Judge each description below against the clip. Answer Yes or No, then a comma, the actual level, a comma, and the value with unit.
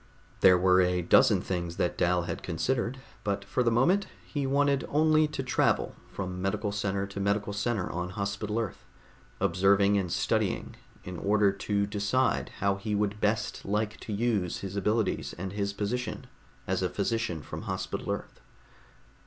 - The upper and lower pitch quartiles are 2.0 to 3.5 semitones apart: Yes, average, 2.8 semitones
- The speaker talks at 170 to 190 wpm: No, average, 160 wpm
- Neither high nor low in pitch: No, low, 100 Hz